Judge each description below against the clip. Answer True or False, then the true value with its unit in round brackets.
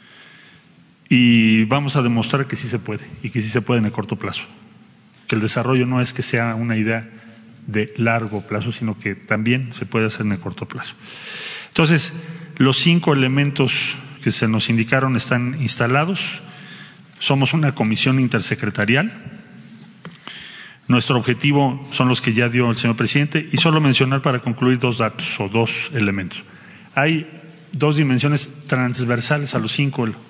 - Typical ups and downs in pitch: True (3.9 semitones)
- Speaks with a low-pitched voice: True (125 Hz)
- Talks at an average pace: True (160 wpm)